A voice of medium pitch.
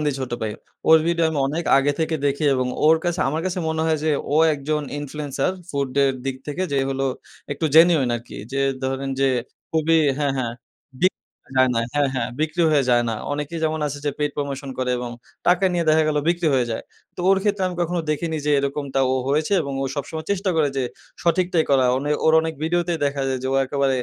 Yes: medium, 150 Hz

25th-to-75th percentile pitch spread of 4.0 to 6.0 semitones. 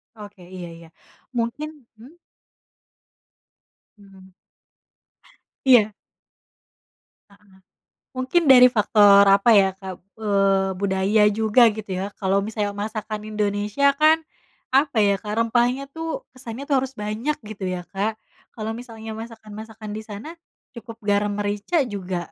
No: average, 2.9 semitones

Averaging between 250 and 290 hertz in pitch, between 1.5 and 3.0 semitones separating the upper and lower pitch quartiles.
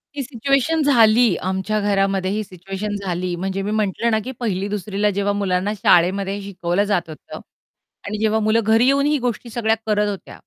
No: high, 205 Hz; narrow, 2.6 semitones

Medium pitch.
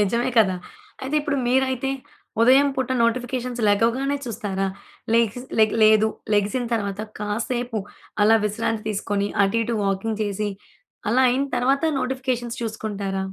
No: high, 230 Hz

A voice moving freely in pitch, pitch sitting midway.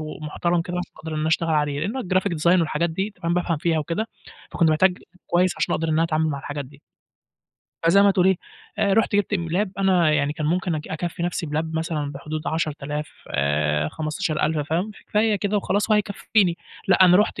No: average, 3.4 semitones; medium, 165 Hz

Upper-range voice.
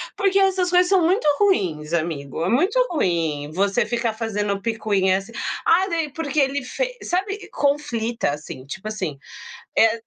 Yes: high, 230 Hz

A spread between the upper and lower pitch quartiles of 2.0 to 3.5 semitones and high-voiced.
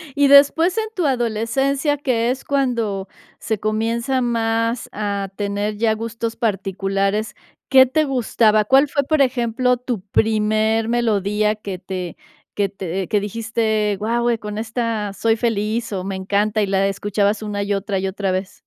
Yes: average, 2.9 semitones; high, 220 Hz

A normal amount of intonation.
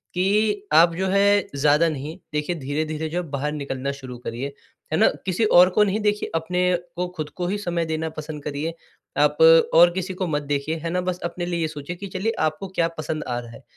Yes: average, 3.6 semitones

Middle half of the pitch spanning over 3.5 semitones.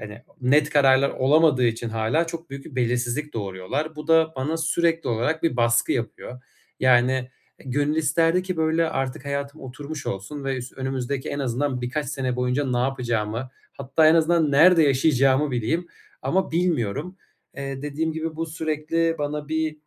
Yes: average, 4.0 semitones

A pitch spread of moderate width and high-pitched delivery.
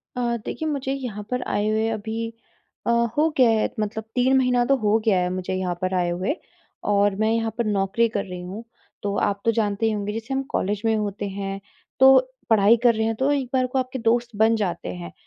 Yes: average, 3.3 semitones; high, 220 Hz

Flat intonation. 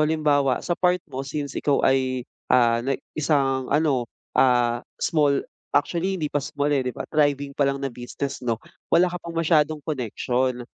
No: average, 3.0 semitones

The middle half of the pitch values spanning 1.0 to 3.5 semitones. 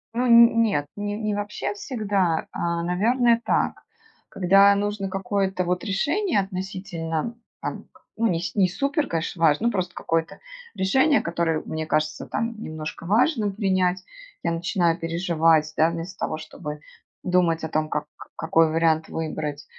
No: average, 4.1 semitones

